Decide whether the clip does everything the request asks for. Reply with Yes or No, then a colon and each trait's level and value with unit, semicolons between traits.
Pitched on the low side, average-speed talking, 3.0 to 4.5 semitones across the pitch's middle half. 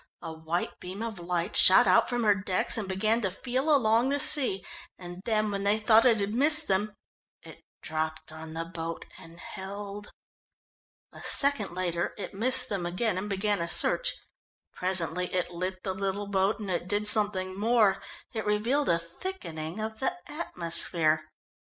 No: high, 200 Hz; average, 170 wpm; average, 3.8 semitones